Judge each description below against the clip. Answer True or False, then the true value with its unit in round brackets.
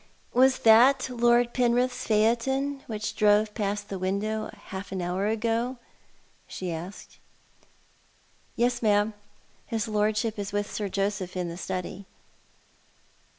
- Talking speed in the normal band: False (130 wpm)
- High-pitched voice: True (215 Hz)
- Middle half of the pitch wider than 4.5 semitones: False (3.1 semitones)